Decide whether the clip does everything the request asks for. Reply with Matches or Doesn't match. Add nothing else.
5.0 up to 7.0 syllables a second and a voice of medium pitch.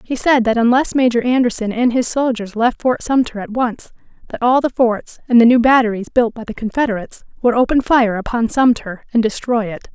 Doesn't match